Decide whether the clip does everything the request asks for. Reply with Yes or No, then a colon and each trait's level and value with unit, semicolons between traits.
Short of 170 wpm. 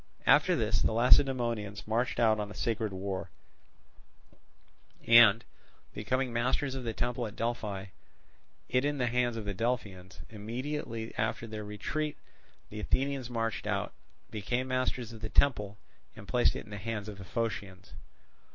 Yes: average, 150 wpm